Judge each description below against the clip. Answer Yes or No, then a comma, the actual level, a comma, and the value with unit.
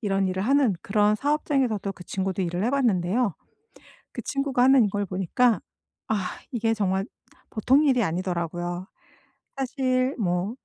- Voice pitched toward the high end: Yes, high, 210 Hz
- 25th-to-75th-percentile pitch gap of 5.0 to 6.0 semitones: Yes, average, 5.3 semitones